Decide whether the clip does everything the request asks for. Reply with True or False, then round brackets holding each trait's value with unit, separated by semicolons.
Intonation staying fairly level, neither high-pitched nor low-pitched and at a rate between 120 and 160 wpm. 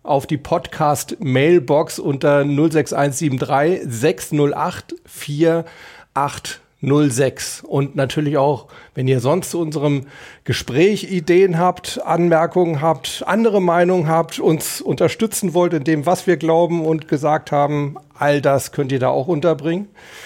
False (3.2 semitones; 155 Hz; 125 wpm)